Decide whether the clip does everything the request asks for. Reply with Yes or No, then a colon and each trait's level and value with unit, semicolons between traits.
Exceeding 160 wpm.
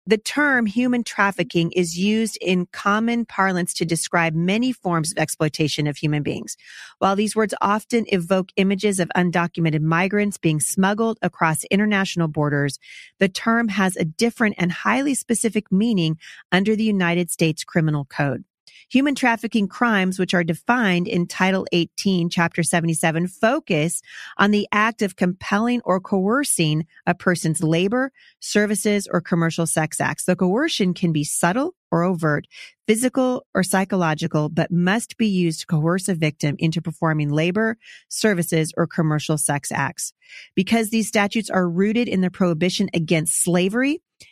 No: average, 150 wpm